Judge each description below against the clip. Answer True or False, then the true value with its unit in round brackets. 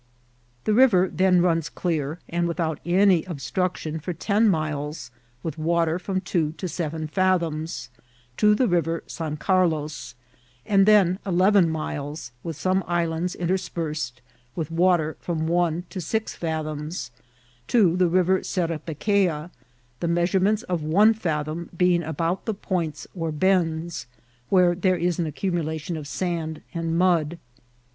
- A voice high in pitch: False (170 Hz)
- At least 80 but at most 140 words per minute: True (135 wpm)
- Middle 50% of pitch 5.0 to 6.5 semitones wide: False (2.7 semitones)